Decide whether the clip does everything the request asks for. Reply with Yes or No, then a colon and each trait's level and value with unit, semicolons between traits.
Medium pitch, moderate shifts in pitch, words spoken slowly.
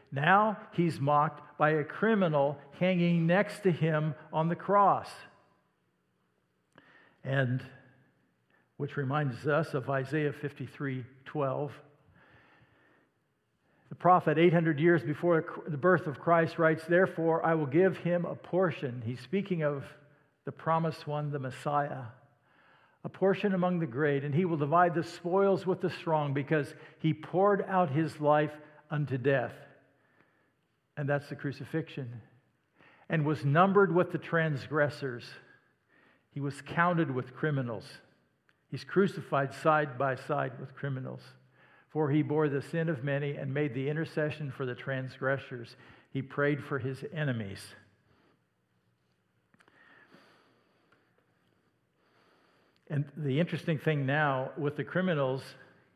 Yes: medium, 150 Hz; average, 3.3 semitones; slow, 125 wpm